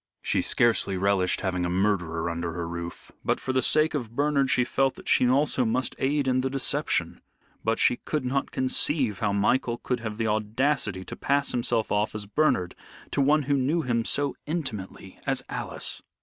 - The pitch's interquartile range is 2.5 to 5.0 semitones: No, wide, 5.4 semitones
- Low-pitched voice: Yes, low, 120 Hz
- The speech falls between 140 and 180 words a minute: No, average, 190 wpm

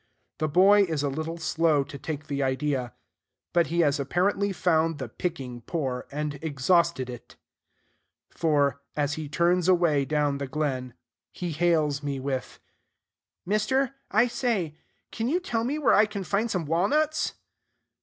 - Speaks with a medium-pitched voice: Yes, medium, 160 Hz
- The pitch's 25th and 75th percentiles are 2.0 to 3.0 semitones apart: No, average, 4.6 semitones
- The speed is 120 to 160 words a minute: Yes, average, 155 wpm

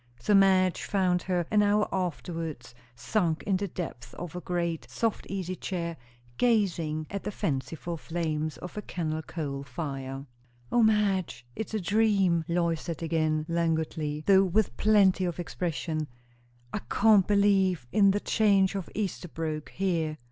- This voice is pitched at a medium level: Yes, medium, 175 Hz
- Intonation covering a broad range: No, average, 3.9 semitones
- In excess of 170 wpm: No, average, 150 wpm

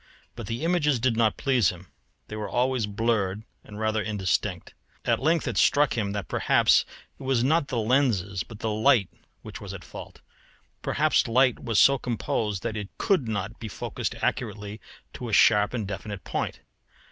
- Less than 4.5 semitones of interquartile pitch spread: Yes, average, 3.7 semitones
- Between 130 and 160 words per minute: No, average, 180 wpm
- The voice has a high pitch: No, low, 110 Hz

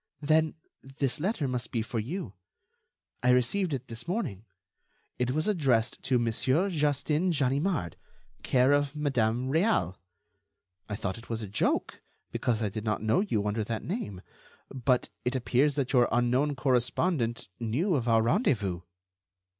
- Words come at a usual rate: Yes, average, 150 wpm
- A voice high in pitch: No, low, 125 Hz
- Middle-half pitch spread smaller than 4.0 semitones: No, average, 4.7 semitones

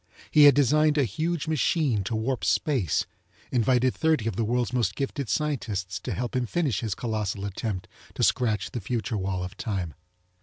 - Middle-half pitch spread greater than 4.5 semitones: Yes, average, 5.2 semitones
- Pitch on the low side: Yes, low, 120 Hz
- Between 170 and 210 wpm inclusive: Yes, average, 180 wpm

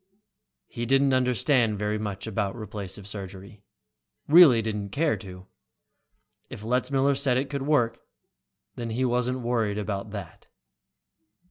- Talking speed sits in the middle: No, slow, 125 wpm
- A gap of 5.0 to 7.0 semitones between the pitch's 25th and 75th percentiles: No, average, 4.0 semitones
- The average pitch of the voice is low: Yes, low, 115 Hz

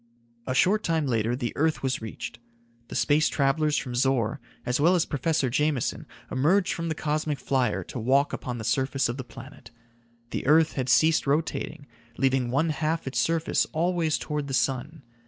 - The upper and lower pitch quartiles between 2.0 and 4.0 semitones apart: Yes, average, 3.6 semitones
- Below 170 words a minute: No, average, 175 wpm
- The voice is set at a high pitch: No, medium, 140 Hz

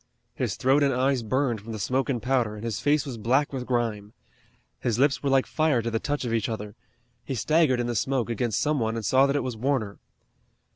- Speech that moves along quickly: Yes, fast, 235 wpm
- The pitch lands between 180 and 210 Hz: No, low, 125 Hz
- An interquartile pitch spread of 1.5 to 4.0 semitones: Yes, average, 3.3 semitones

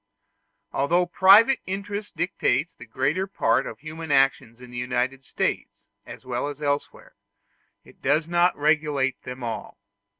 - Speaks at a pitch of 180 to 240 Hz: No, medium, 145 Hz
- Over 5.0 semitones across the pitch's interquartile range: Yes, wide, 5.4 semitones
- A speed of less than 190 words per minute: Yes, average, 140 wpm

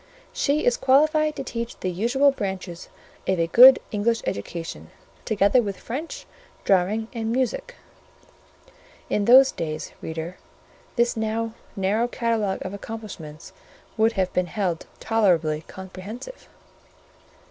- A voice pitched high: Yes, high, 220 Hz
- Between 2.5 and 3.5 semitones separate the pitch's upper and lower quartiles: No, average, 4.6 semitones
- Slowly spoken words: Yes, slow, 120 wpm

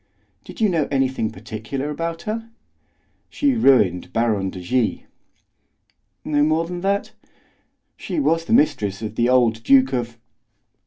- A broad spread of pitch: Yes, wide, 6.8 semitones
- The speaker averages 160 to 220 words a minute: No, average, 140 wpm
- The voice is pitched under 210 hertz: Yes, low, 135 Hz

